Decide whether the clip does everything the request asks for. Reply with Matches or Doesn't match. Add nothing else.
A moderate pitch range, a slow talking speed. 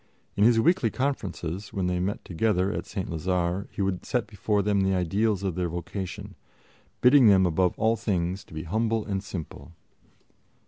Doesn't match